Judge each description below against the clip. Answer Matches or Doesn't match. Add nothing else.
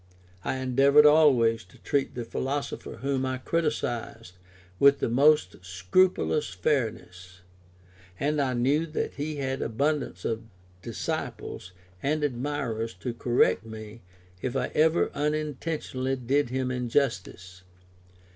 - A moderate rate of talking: Doesn't match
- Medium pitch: Doesn't match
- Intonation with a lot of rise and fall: Doesn't match